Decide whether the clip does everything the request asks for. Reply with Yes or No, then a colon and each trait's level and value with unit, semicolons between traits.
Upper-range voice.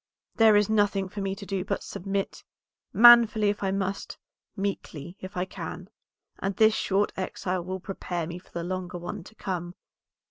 Yes: high, 195 Hz